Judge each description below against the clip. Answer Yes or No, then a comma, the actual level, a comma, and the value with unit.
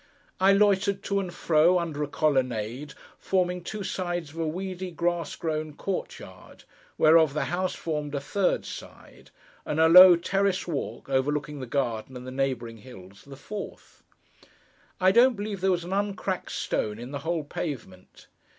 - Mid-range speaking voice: Yes, medium, 165 Hz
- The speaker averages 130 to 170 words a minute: Yes, average, 165 wpm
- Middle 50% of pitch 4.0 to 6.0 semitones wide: Yes, average, 5.1 semitones